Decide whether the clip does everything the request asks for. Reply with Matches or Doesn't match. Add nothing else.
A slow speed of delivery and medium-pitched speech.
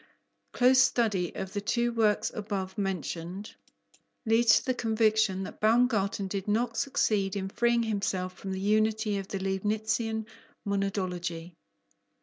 Doesn't match